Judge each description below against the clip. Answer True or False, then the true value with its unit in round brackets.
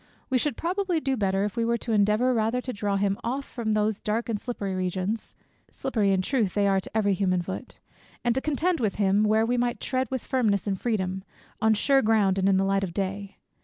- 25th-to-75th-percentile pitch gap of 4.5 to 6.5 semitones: False (3.8 semitones)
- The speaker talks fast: True (230 wpm)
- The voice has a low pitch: False (215 Hz)